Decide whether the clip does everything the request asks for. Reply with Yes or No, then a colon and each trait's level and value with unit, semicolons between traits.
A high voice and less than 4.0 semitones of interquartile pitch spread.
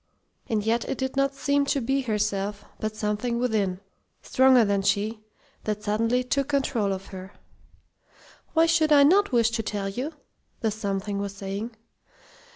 No: high, 225 Hz; average, 4.6 semitones